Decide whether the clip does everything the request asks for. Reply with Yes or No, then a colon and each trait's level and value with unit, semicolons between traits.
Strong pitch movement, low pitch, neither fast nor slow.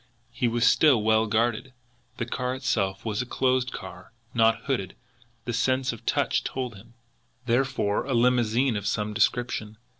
No: average, 2.7 semitones; low, 120 Hz; average, 155 wpm